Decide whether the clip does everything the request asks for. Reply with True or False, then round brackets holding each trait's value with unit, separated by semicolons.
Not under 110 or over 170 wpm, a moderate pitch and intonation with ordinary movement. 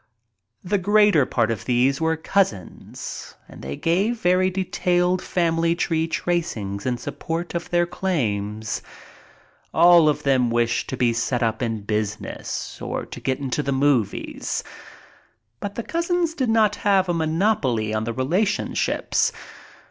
False (145 wpm; 160 Hz; 7.6 semitones)